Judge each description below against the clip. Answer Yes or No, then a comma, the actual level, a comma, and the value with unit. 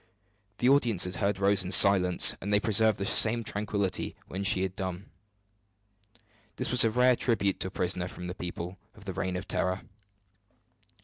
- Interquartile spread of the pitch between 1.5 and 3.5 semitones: Yes, average, 2.8 semitones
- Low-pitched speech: Yes, low, 100 Hz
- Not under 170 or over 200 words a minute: Yes, average, 180 wpm